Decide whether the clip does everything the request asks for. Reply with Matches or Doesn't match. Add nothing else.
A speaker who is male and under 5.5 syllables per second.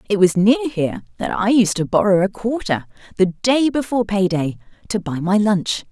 Doesn't match